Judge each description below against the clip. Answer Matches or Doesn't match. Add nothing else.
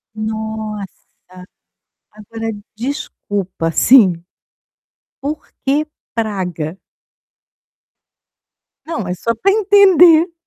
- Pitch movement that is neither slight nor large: Doesn't match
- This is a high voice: Matches